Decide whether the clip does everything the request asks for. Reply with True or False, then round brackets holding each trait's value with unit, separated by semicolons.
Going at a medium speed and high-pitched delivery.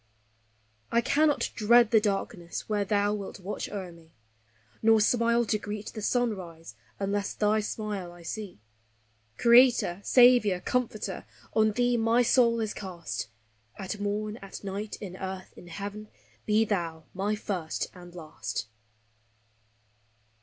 False (130 wpm; 210 Hz)